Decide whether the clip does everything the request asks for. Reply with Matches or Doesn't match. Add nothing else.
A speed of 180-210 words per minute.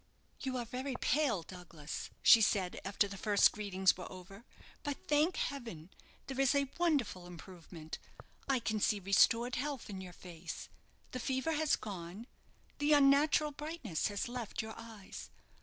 Doesn't match